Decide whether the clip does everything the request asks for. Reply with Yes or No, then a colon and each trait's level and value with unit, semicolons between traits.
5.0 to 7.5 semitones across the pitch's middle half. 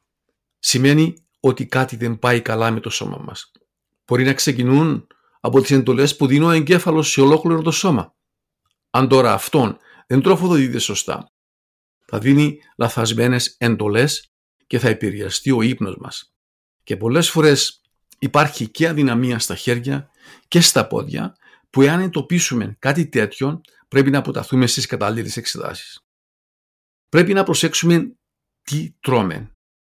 No: average, 4.6 semitones